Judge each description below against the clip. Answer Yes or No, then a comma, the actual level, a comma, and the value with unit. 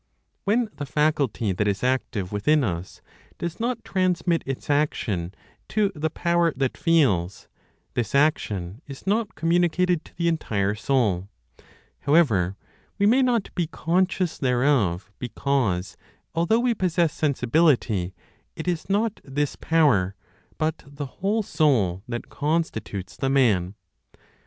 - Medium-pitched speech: Yes, medium, 145 Hz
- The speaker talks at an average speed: No, slow, 130 wpm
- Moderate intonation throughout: No, wide, 8.3 semitones